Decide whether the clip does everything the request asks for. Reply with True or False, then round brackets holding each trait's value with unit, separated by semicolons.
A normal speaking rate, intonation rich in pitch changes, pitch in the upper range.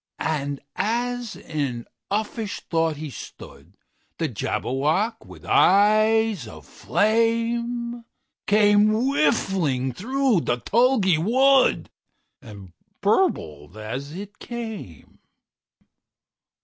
False (75 wpm; 8.4 semitones; 205 Hz)